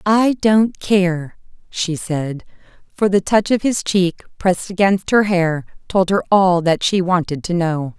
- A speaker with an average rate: Yes, average, 175 wpm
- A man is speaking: No, female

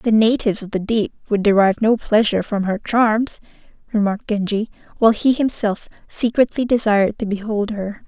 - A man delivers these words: No, female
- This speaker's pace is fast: No, average, 165 wpm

